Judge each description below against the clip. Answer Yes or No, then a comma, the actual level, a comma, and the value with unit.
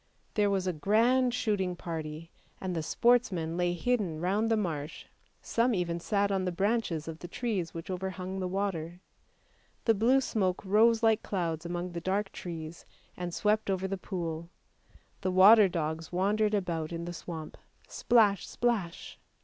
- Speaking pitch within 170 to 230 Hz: Yes, medium, 185 Hz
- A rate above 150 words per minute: Yes, average, 160 wpm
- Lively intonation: No, average, 3.8 semitones